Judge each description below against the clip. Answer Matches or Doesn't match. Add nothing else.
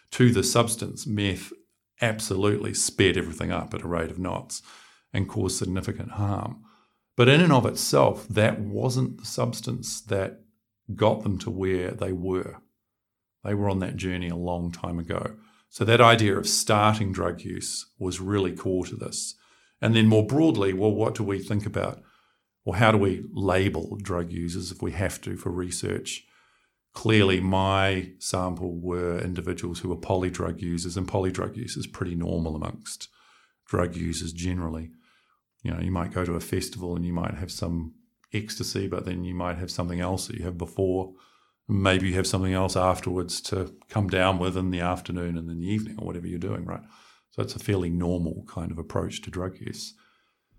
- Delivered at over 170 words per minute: Matches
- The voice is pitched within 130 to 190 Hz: Doesn't match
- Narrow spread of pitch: Doesn't match